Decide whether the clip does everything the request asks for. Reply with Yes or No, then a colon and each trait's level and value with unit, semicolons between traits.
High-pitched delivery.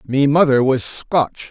No: low, 135 Hz